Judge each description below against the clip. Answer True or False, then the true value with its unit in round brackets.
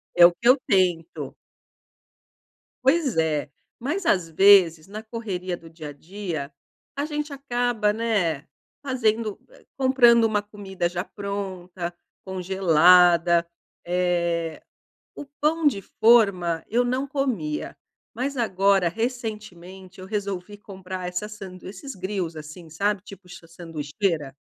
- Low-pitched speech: False (190 Hz)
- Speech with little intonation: False (4.6 semitones)